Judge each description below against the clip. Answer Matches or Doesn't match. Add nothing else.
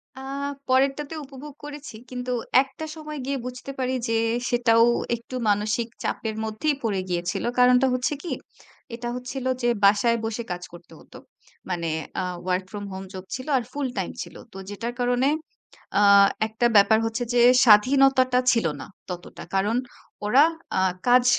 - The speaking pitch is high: Matches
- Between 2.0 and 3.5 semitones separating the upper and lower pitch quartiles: Doesn't match